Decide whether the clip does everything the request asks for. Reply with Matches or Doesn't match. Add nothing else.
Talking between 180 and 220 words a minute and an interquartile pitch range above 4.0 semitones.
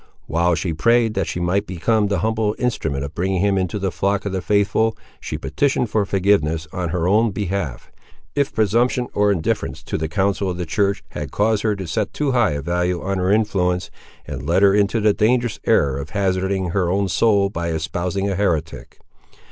Doesn't match